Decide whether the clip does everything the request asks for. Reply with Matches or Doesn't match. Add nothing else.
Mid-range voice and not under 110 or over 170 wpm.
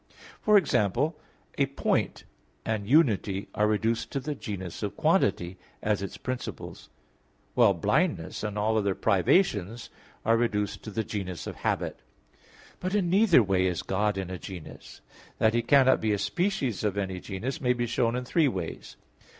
Doesn't match